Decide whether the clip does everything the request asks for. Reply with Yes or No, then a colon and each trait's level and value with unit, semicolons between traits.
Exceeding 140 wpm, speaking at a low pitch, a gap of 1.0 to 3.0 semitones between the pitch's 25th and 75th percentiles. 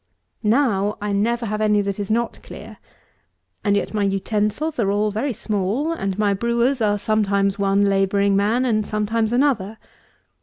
No: average, 160 wpm; high, 210 Hz; narrow, 2.5 semitones